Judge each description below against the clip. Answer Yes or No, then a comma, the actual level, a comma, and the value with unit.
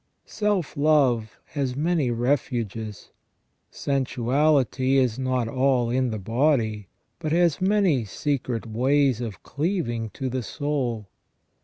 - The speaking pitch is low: Yes, low, 130 Hz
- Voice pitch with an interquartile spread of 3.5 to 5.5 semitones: Yes, average, 3.8 semitones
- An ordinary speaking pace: No, slow, 120 wpm